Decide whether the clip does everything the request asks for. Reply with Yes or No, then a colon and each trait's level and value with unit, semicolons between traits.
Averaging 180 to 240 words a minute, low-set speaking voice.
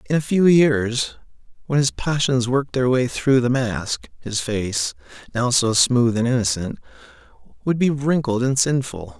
No: average, 165 wpm; low, 125 Hz